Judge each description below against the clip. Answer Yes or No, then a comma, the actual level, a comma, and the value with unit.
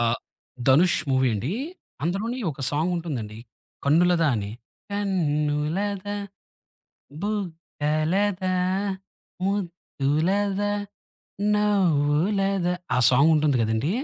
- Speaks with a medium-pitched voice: Yes, medium, 170 Hz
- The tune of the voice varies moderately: Yes, average, 5.0 semitones